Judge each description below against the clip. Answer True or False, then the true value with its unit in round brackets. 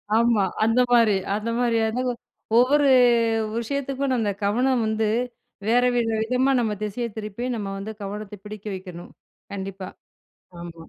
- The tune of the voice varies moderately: True (3.3 semitones)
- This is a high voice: True (225 Hz)